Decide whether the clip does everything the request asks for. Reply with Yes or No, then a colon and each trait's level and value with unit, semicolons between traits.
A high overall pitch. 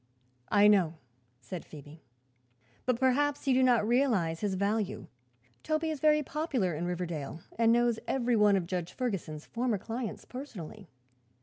Yes: high, 215 Hz